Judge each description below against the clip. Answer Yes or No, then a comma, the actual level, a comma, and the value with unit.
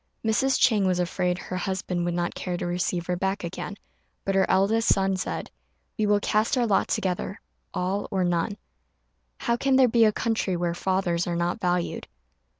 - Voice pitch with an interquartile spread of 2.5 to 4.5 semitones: Yes, average, 2.8 semitones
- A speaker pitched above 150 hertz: Yes, high, 190 Hz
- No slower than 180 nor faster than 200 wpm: Yes, average, 185 wpm